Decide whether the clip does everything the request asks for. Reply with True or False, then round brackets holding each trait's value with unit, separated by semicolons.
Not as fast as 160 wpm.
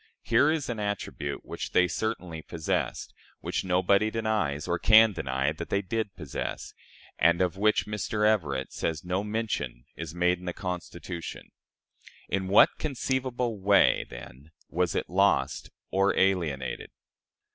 True (140 wpm)